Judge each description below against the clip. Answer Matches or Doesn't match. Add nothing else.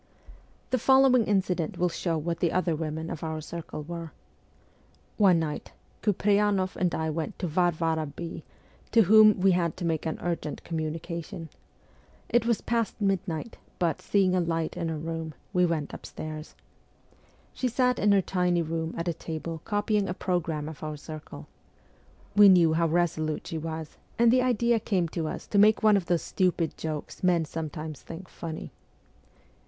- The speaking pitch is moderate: Matches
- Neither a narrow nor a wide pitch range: Matches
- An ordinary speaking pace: Matches